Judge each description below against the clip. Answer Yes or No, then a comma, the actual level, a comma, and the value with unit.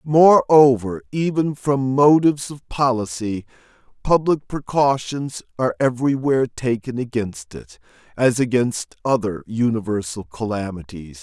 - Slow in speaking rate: Yes, slow, 95 wpm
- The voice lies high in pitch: No, low, 125 Hz